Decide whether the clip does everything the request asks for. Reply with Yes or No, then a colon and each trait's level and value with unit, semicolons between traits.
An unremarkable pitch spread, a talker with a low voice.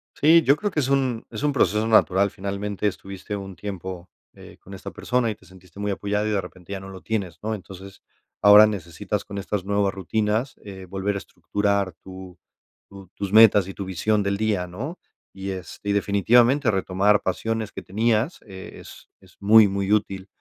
No: narrow, 2.2 semitones; low, 100 Hz